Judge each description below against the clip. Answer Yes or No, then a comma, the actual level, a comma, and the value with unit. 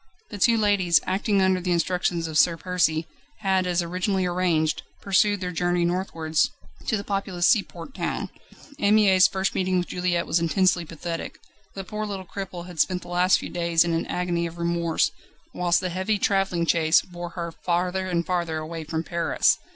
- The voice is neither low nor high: Yes, medium, 180 Hz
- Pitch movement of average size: No, narrow, 1.9 semitones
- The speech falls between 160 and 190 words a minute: Yes, average, 180 wpm